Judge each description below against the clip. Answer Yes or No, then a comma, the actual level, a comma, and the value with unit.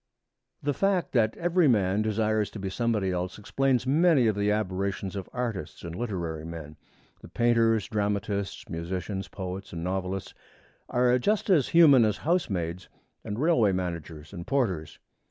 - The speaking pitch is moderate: No, low, 105 Hz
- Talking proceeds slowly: No, average, 150 wpm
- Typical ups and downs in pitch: Yes, average, 5.0 semitones